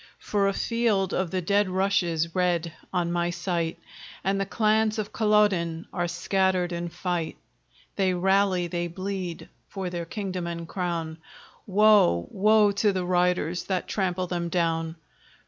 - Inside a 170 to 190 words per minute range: No, average, 145 wpm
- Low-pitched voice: No, medium, 180 Hz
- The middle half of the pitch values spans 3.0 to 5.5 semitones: No, narrow, 2.4 semitones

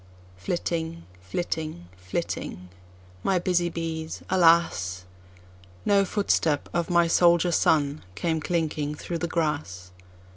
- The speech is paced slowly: Yes, slow, 100 wpm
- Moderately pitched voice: Yes, medium, 160 Hz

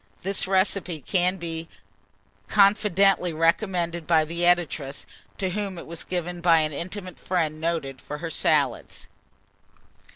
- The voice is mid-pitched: Yes, medium, 170 Hz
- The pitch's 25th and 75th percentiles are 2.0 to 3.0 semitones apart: Yes, narrow, 2.5 semitones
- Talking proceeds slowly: Yes, slow, 130 wpm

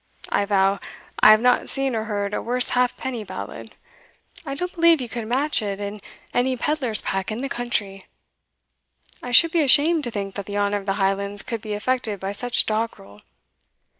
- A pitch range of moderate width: Yes, average, 4.1 semitones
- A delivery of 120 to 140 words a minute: No, average, 190 wpm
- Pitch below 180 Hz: No, high, 220 Hz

